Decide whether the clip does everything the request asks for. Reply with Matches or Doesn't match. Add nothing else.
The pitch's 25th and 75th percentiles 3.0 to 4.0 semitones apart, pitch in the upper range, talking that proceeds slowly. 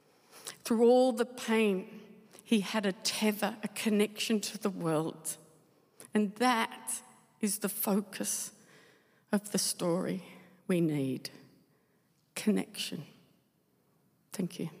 Matches